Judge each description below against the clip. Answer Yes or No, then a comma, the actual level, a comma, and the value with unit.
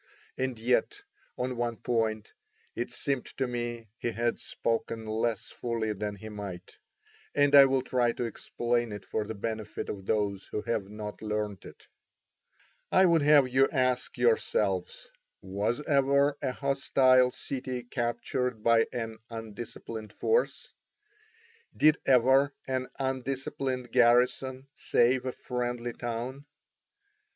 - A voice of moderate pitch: No, low, 120 Hz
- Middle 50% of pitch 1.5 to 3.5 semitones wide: Yes, average, 3.0 semitones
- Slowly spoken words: Yes, slow, 130 wpm